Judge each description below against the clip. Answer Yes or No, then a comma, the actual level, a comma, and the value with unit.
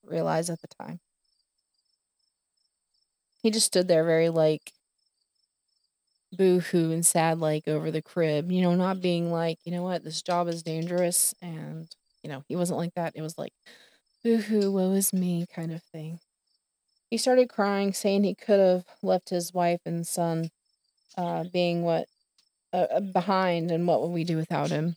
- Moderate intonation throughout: No, narrow, 2.2 semitones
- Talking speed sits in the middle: Yes, average, 170 wpm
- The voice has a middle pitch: Yes, medium, 170 Hz